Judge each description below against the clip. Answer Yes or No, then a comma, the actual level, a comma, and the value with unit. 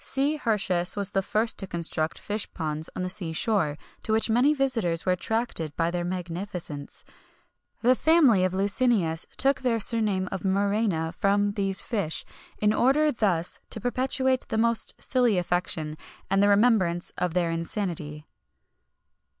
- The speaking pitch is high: Yes, high, 200 Hz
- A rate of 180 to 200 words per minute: No, average, 155 wpm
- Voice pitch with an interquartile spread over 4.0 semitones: Yes, average, 4.8 semitones